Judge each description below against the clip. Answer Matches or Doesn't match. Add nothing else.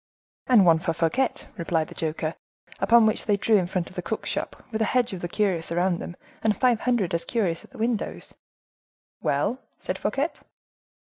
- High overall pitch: Matches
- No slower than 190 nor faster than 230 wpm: Matches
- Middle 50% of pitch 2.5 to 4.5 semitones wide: Doesn't match